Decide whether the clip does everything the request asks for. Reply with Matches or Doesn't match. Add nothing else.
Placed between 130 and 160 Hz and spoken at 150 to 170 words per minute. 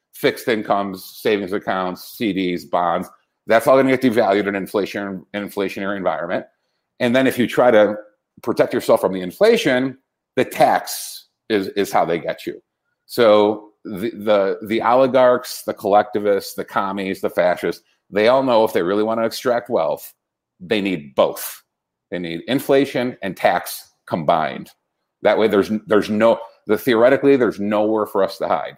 Doesn't match